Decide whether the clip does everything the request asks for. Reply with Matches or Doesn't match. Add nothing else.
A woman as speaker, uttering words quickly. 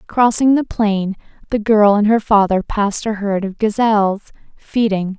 Doesn't match